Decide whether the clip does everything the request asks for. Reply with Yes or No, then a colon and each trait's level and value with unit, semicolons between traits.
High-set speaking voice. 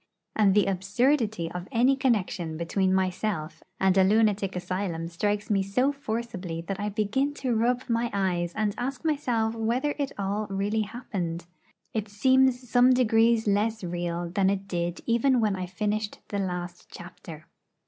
Yes: high, 205 Hz